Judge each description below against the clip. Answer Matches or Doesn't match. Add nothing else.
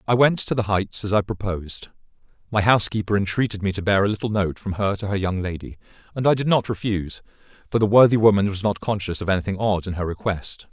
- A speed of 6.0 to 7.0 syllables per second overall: Matches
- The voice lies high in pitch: Doesn't match